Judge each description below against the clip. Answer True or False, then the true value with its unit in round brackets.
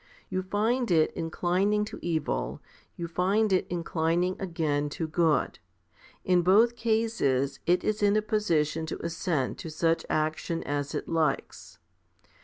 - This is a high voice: False (170 Hz)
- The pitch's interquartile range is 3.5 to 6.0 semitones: True (4.5 semitones)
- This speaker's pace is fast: False (140 wpm)